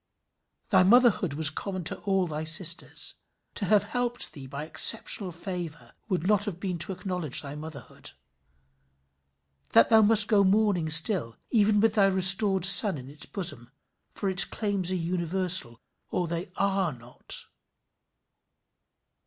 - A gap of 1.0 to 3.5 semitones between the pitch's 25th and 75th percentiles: No, average, 4.2 semitones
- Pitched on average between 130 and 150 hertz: No, medium, 185 Hz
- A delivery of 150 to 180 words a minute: No, average, 140 wpm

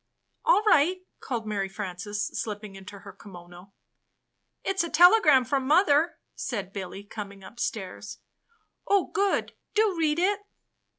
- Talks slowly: Yes, slow, 130 wpm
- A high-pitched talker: Yes, high, 230 Hz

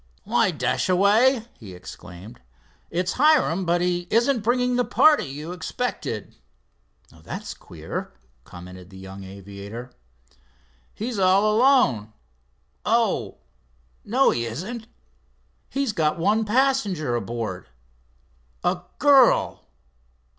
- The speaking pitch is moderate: Yes, medium, 170 Hz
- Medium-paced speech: No, slow, 95 wpm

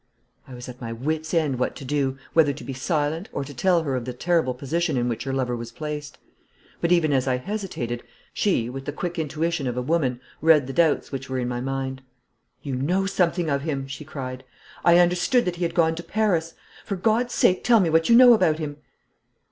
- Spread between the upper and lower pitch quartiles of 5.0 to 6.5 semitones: No, average, 4.6 semitones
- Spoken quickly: Yes, fast, 225 wpm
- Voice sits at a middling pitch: Yes, medium, 150 Hz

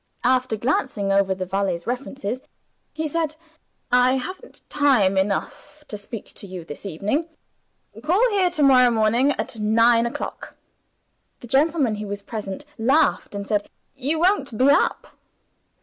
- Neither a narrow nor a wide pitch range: No, wide, 5.9 semitones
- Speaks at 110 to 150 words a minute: Yes, average, 145 wpm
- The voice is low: No, high, 240 Hz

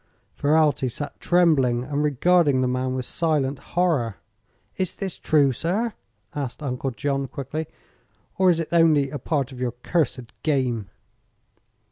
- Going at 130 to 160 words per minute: Yes, average, 140 wpm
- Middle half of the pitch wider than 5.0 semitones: No, average, 4.1 semitones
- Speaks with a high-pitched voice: No, medium, 145 Hz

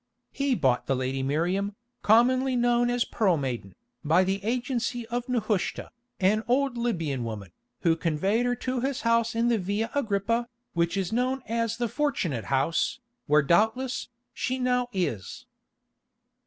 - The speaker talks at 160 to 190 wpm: No, average, 150 wpm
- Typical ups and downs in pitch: No, wide, 6.6 semitones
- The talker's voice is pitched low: No, high, 220 Hz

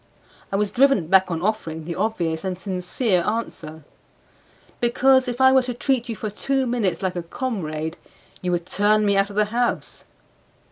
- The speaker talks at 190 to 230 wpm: No, average, 180 wpm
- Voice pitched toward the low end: No, high, 205 Hz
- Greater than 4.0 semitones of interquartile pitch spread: Yes, average, 5.3 semitones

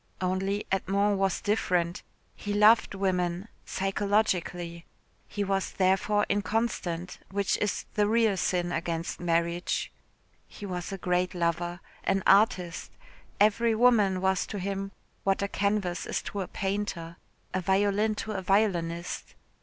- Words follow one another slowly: Yes, slow, 130 wpm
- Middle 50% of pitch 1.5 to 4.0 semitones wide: Yes, narrow, 2.5 semitones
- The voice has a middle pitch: No, high, 195 Hz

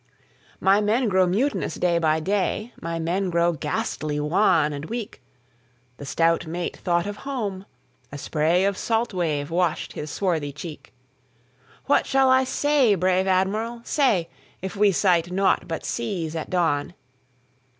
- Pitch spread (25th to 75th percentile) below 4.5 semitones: No, average, 4.8 semitones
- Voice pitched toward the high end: No, medium, 175 Hz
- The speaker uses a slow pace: Yes, slow, 130 wpm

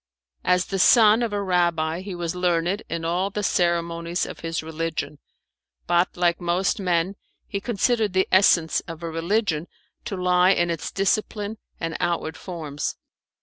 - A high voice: No, medium, 175 Hz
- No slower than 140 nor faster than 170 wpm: Yes, average, 155 wpm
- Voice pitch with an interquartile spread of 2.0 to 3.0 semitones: Yes, average, 2.7 semitones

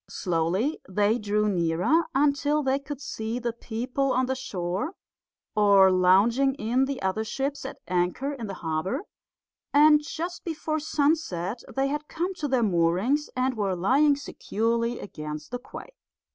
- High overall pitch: Yes, high, 245 Hz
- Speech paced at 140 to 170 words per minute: Yes, average, 150 wpm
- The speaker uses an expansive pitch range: Yes, wide, 6.7 semitones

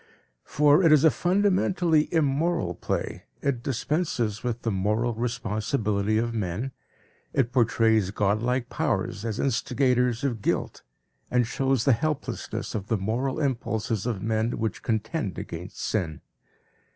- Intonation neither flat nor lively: Yes, average, 4.2 semitones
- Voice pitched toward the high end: No, low, 120 Hz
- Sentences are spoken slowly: Yes, slow, 130 wpm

